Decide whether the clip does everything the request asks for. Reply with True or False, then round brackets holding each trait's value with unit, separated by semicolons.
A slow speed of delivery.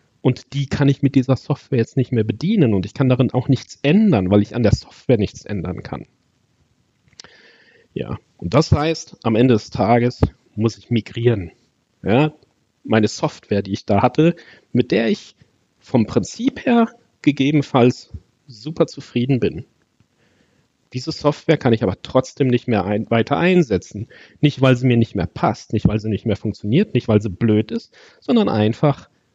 False (175 wpm)